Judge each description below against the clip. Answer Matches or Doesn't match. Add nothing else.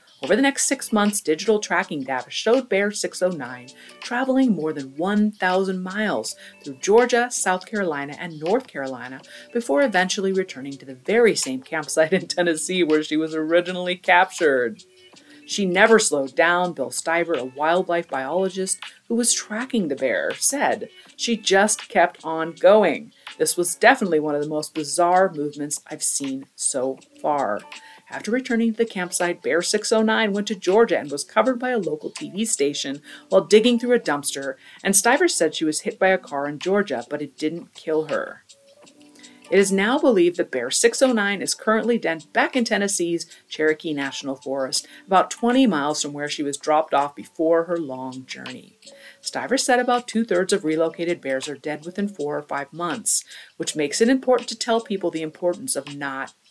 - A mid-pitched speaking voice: Matches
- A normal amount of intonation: Doesn't match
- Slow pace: Doesn't match